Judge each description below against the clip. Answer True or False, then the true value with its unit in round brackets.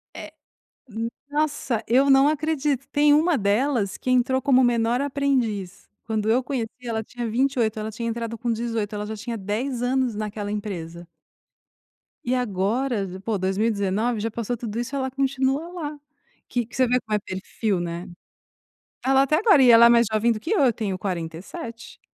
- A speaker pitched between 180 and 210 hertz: False (235 Hz)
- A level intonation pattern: False (3.9 semitones)